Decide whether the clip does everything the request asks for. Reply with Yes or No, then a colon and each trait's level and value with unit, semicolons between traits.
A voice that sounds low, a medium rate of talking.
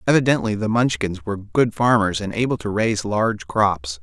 Yes: low, 105 Hz; average, 180 wpm